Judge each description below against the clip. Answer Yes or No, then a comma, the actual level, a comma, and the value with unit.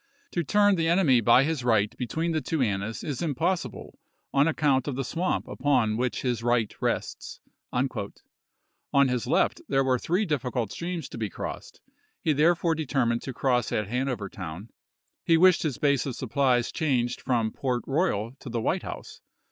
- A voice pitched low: Yes, low, 130 Hz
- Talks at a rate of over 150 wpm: Yes, average, 180 wpm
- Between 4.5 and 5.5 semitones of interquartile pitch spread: Yes, average, 4.9 semitones